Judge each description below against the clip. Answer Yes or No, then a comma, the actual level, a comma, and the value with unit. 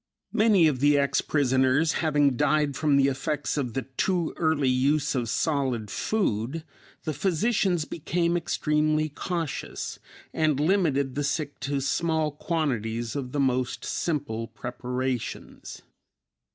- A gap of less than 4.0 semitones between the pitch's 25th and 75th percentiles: Yes, average, 3.5 semitones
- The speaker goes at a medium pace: No, slow, 125 wpm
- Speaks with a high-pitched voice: No, medium, 145 Hz